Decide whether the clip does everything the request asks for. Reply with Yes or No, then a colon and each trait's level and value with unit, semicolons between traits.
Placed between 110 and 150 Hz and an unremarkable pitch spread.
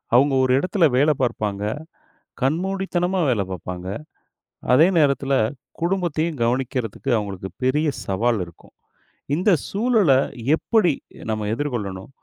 No: low, 135 Hz; wide, 7.8 semitones